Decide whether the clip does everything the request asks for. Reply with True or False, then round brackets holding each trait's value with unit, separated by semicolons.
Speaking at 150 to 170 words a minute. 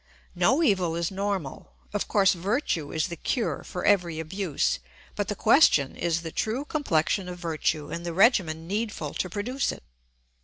True (165 wpm)